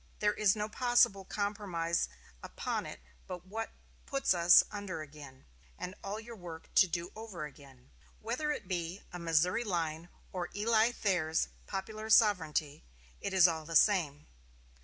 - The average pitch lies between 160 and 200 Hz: Yes, medium, 185 Hz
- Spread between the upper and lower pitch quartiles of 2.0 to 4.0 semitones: No, average, 4.5 semitones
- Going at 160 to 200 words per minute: No, average, 150 wpm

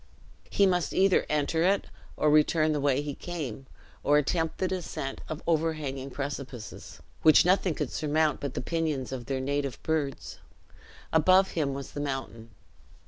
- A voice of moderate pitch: Yes, medium, 150 Hz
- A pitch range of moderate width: Yes, average, 3.0 semitones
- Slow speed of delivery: No, average, 155 wpm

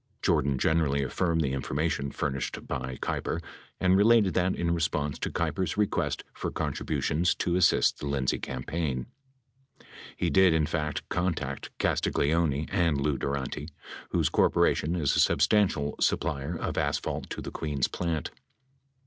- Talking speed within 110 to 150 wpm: Yes, average, 140 wpm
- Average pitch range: Yes, average, 3.6 semitones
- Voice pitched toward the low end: Yes, very low, 80 Hz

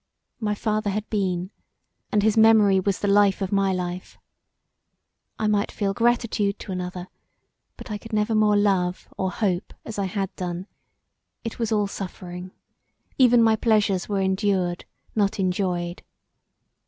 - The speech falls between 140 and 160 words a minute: Yes, average, 150 wpm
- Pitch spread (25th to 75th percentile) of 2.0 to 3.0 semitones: Yes, narrow, 2.4 semitones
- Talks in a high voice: Yes, high, 200 Hz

